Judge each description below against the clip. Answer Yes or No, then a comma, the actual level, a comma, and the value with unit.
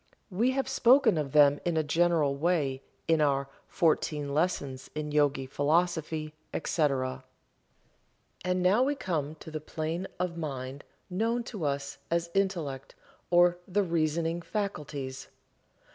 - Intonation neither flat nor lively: Yes, average, 3.9 semitones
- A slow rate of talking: Yes, slow, 130 wpm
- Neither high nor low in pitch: Yes, medium, 160 Hz